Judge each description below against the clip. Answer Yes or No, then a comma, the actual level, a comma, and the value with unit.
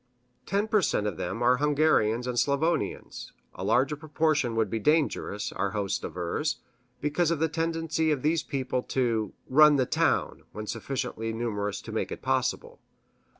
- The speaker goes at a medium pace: Yes, average, 160 wpm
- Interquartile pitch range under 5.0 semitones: No, wide, 5.6 semitones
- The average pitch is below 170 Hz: Yes, low, 135 Hz